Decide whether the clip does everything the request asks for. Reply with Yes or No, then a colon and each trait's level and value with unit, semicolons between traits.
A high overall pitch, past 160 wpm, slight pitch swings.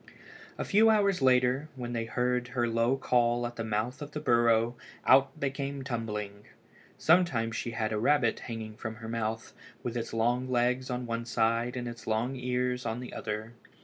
No: low, 120 Hz; average, 185 wpm; narrow, 2.1 semitones